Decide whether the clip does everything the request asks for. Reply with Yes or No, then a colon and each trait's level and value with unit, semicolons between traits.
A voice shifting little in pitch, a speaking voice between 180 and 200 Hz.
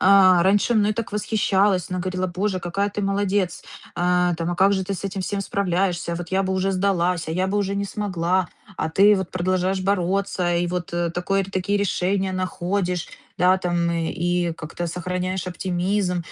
Yes: narrow, 2.0 semitones; medium, 185 Hz